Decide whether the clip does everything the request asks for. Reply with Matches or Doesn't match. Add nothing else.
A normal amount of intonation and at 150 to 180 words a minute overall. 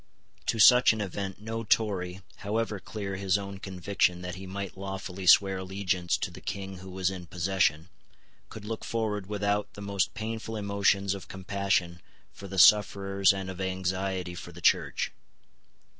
Doesn't match